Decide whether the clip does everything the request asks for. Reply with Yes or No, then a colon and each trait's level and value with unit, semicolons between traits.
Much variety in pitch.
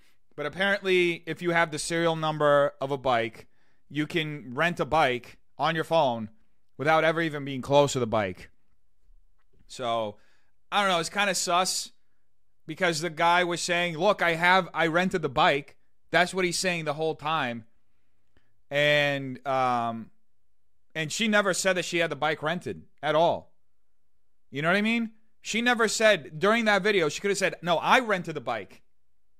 Yes: wide, 6.4 semitones